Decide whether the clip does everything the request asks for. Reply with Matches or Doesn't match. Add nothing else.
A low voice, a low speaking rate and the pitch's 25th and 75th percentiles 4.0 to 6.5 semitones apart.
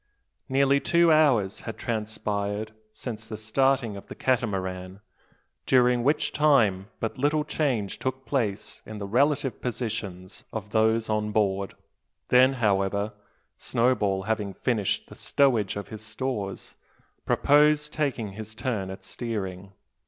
Matches